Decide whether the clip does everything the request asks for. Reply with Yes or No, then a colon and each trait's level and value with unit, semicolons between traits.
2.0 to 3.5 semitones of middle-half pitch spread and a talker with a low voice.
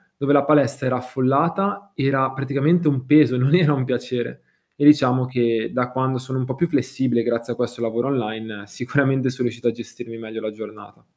Yes: average, 2.7 semitones; low, 130 Hz